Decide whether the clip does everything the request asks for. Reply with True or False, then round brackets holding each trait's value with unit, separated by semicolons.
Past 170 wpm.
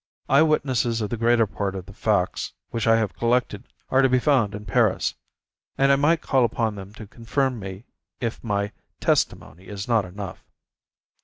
True (180 wpm)